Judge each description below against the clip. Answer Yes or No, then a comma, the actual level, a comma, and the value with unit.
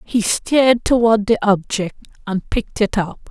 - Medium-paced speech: Yes, average, 165 wpm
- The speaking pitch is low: No, high, 215 Hz